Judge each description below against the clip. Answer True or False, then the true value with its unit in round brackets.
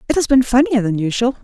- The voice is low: False (245 Hz)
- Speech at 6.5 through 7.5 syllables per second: True (6.6 syllables/s)